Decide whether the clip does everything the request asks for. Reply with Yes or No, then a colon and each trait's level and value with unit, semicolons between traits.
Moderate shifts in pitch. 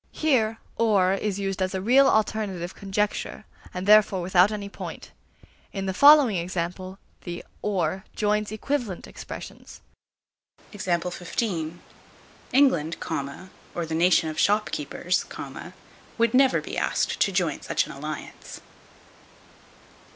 Yes: average, 3.3 semitones